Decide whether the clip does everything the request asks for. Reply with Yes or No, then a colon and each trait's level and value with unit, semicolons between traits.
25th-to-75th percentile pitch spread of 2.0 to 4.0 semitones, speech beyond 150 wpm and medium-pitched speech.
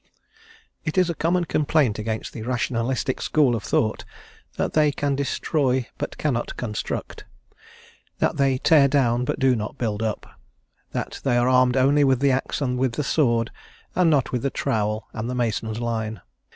No: average, 3.4 semitones; average, 175 wpm; low, 125 Hz